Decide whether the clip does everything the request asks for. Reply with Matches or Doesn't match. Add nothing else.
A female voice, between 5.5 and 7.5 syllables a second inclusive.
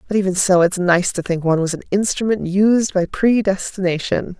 Doesn't match